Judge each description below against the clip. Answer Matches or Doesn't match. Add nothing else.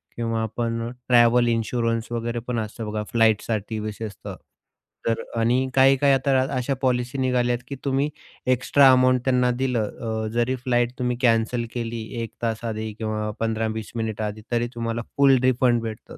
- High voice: Doesn't match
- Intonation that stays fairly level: Matches